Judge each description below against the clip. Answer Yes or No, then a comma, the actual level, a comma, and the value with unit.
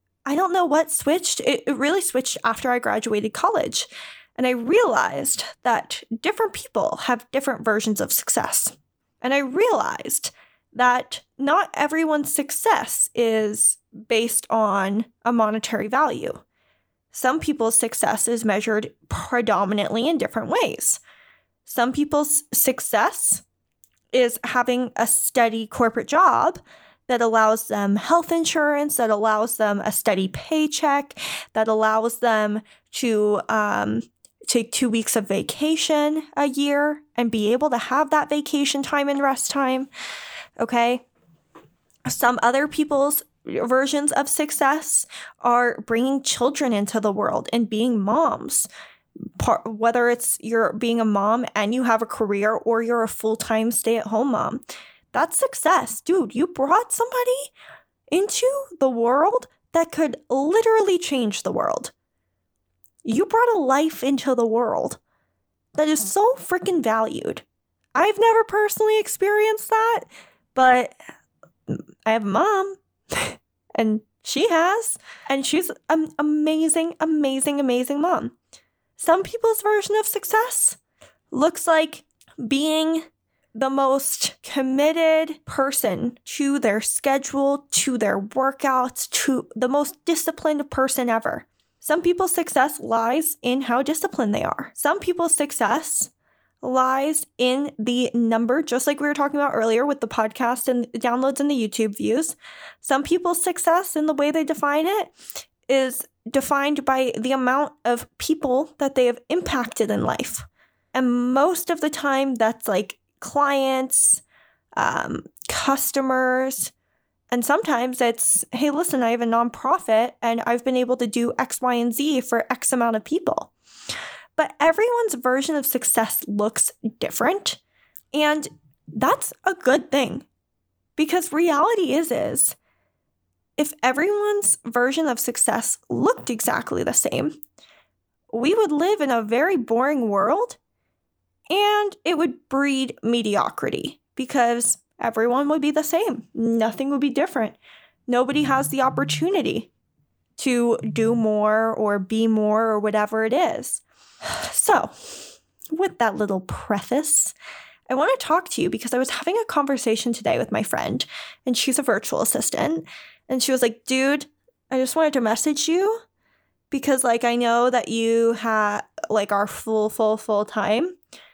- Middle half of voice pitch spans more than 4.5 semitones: Yes, average, 5.1 semitones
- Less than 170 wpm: Yes, average, 140 wpm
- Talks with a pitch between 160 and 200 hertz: No, very high, 265 Hz